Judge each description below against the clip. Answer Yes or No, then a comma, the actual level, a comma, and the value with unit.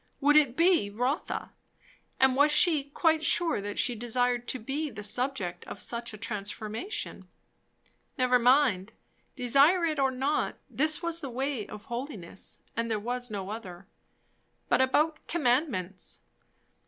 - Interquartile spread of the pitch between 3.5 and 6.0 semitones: Yes, average, 5.3 semitones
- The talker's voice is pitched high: Yes, very high, 250 Hz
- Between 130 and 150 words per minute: Yes, average, 140 wpm